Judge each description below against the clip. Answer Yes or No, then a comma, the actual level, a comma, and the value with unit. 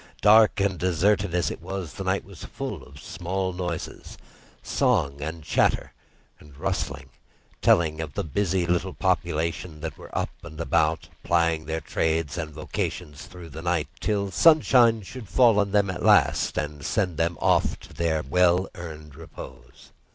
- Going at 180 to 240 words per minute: No, average, 160 wpm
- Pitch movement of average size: Yes, average, 3.6 semitones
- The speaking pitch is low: Yes, very low, 85 Hz